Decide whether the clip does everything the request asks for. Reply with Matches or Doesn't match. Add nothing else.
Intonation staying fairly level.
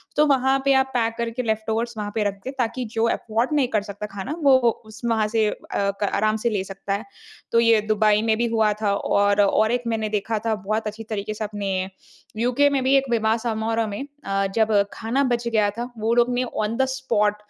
Matches